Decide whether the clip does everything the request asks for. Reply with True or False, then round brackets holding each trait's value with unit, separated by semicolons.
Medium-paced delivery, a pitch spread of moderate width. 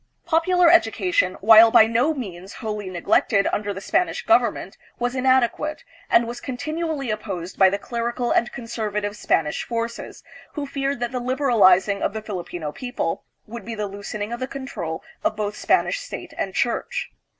True (165 wpm; 4.3 semitones)